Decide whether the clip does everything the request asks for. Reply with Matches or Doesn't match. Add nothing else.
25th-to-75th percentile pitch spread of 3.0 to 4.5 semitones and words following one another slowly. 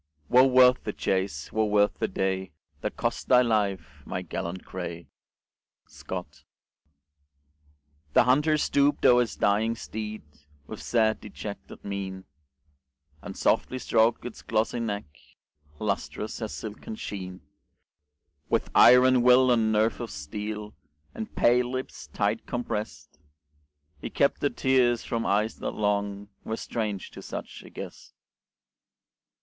Matches